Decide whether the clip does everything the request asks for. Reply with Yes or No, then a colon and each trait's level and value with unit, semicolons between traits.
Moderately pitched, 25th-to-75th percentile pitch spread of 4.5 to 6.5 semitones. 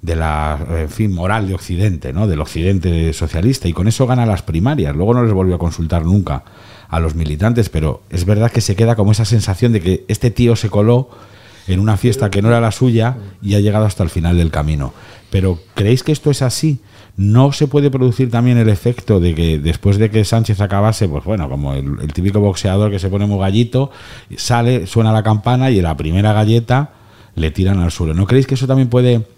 No: low, 105 Hz; average, 4.9 semitones